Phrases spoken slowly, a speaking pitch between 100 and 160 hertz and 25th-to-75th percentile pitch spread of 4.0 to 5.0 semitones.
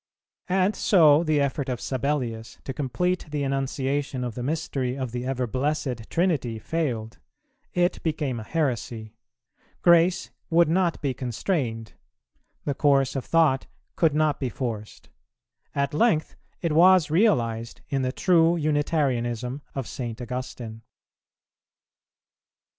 Yes: slow, 125 wpm; medium, 140 Hz; average, 4.6 semitones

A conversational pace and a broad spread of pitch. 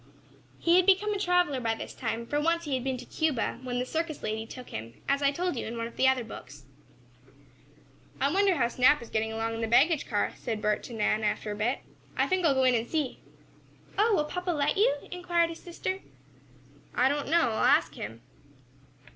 No: fast, 220 wpm; wide, 6.7 semitones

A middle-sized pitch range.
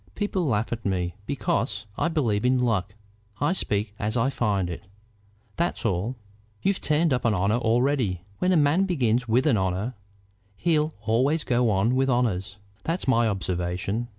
No: wide, 5.7 semitones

